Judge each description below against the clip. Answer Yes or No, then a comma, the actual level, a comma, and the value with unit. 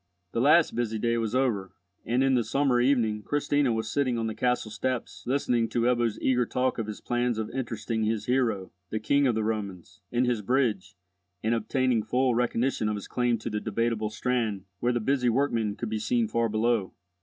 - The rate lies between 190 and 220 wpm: Yes, average, 200 wpm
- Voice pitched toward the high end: No, low, 115 Hz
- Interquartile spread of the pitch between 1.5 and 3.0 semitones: Yes, narrow, 2.5 semitones